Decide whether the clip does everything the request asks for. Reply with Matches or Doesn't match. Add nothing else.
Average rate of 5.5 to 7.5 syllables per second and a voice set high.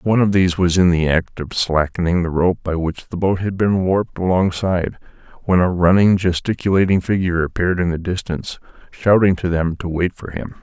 Doesn't match